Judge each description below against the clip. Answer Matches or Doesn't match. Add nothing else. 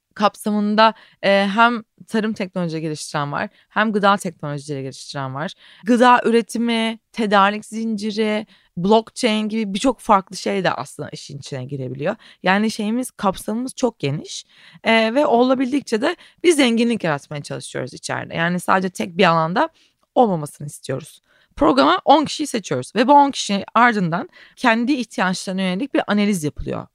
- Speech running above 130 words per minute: Matches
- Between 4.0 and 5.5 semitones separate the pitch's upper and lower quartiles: Matches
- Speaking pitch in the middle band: Doesn't match